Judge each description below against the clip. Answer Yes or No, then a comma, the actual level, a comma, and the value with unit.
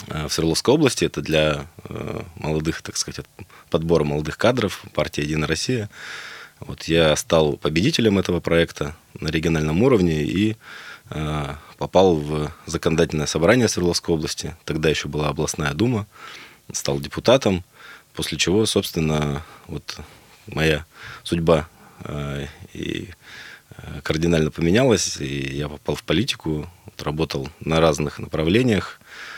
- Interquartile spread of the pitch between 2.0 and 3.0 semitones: Yes, narrow, 2.6 semitones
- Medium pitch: No, very low, 80 Hz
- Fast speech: No, slow, 110 wpm